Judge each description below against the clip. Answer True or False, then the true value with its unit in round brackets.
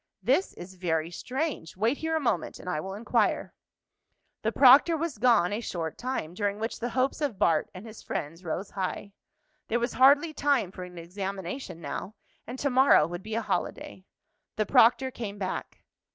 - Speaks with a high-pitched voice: True (215 Hz)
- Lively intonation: True (6.2 semitones)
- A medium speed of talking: True (180 wpm)